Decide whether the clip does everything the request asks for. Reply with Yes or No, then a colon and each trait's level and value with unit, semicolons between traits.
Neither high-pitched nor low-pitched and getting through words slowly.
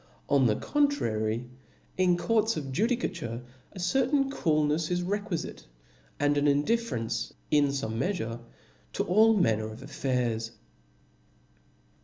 Yes: medium, 150 Hz; slow, 125 wpm